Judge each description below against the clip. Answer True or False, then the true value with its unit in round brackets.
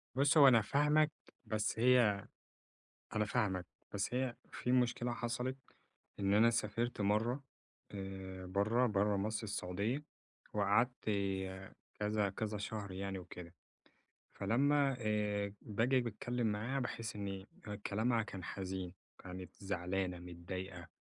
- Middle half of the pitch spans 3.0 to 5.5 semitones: True (3.8 semitones)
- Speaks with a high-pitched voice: False (105 Hz)